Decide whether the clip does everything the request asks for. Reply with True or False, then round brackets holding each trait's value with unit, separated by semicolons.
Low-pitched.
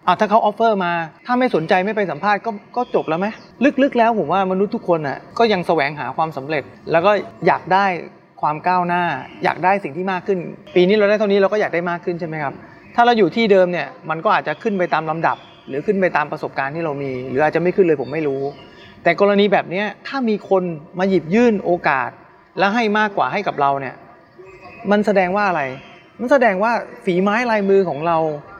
False (190 Hz)